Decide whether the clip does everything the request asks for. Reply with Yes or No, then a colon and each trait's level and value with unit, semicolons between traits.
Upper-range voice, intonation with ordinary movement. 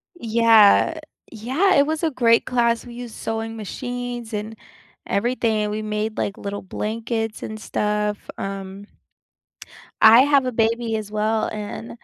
No: high, 225 Hz; narrow, 2.2 semitones